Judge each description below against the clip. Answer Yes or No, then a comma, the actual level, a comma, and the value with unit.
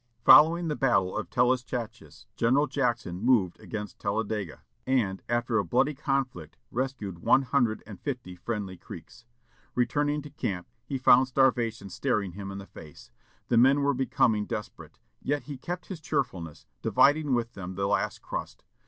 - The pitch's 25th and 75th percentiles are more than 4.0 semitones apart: Yes, average, 5.3 semitones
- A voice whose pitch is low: Yes, low, 120 Hz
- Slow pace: No, average, 155 wpm